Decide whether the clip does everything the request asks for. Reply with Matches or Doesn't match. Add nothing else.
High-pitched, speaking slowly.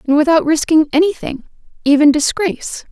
Matches